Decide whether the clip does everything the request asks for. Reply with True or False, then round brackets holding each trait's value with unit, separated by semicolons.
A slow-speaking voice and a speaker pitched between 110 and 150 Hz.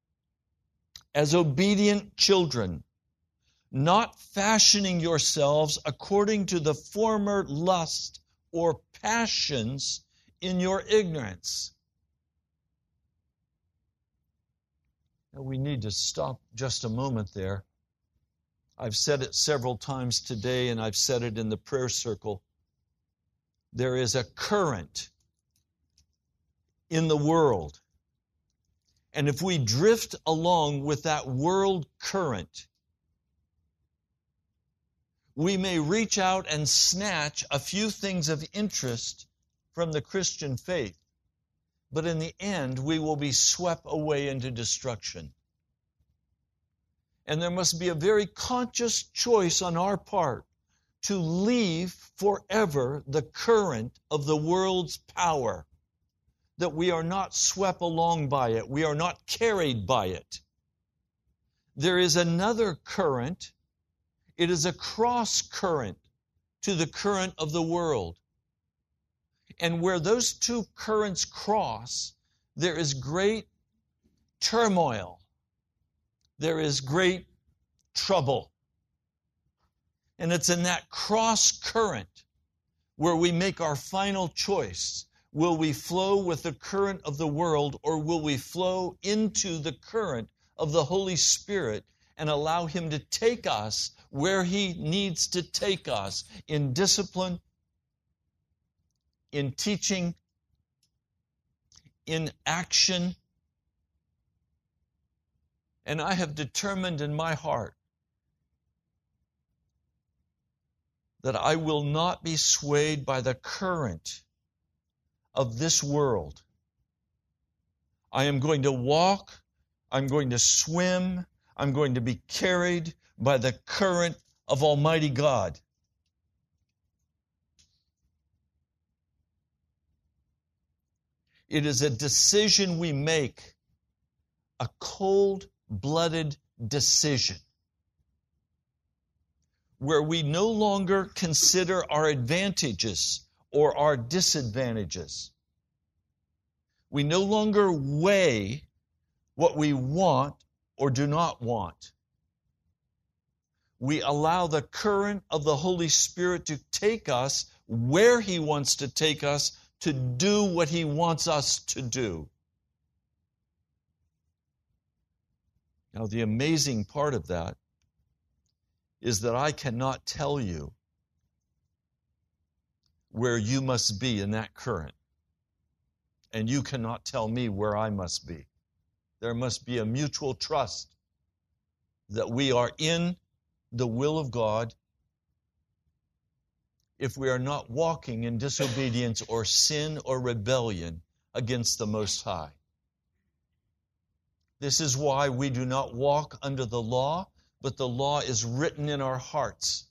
True (110 wpm; 140 Hz)